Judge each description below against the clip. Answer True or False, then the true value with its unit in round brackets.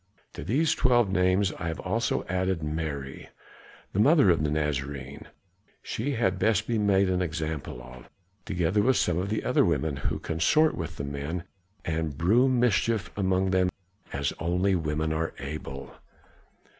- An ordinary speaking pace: True (155 wpm)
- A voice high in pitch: False (90 Hz)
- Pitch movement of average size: True (4.9 semitones)